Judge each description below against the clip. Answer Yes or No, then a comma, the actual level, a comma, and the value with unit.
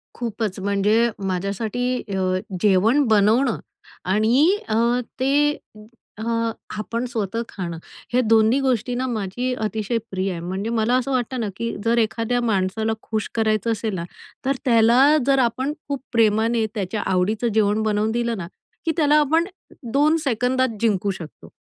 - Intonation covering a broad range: No, average, 3.2 semitones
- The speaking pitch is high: Yes, high, 225 Hz